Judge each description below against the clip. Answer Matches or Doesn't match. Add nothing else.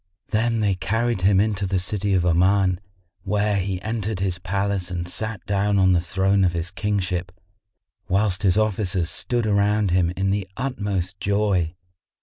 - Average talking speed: Matches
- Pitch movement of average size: Doesn't match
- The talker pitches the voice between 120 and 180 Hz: Doesn't match